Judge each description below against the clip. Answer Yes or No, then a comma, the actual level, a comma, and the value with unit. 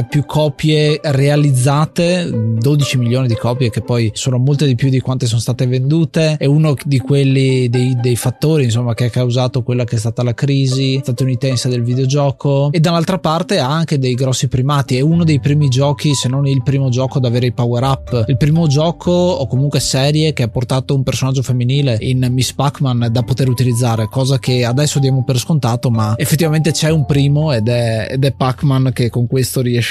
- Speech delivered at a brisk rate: Yes, fast, 200 wpm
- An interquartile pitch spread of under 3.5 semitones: Yes, narrow, 2.6 semitones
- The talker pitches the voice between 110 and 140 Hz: Yes, low, 135 Hz